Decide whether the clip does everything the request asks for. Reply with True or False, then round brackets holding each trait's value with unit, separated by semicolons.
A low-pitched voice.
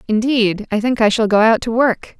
False (225 Hz)